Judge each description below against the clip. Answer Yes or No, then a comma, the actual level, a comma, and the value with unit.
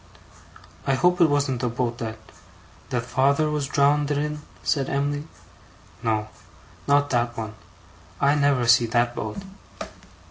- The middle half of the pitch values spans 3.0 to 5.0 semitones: Yes, average, 3.4 semitones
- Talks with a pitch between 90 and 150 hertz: Yes, low, 135 Hz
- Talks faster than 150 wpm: No, average, 140 wpm